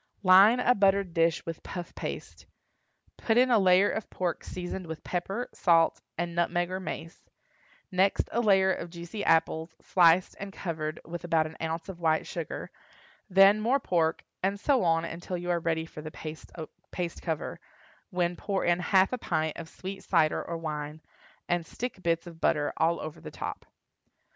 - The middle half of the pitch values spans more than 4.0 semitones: No, average, 2.7 semitones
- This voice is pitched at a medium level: Yes, medium, 175 Hz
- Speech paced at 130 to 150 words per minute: No, average, 175 wpm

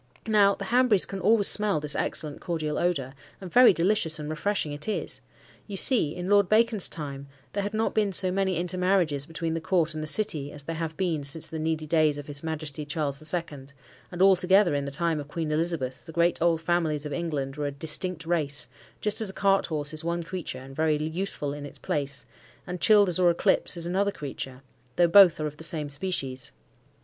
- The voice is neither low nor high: Yes, medium, 165 Hz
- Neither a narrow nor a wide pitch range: Yes, average, 4.1 semitones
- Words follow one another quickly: Yes, fast, 215 wpm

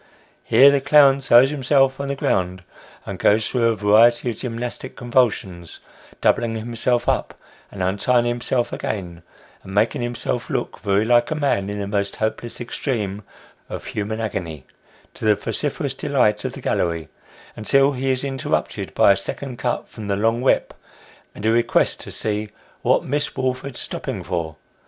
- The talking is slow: No, average, 165 wpm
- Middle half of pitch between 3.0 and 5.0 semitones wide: Yes, average, 4.1 semitones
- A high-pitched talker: No, low, 115 Hz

